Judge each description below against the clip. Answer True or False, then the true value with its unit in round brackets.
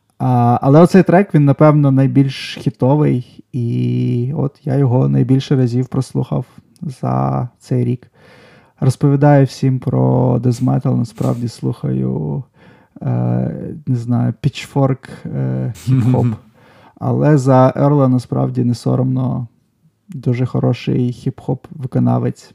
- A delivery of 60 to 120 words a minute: True (105 wpm)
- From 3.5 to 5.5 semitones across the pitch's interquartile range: False (2.7 semitones)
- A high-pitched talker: False (125 Hz)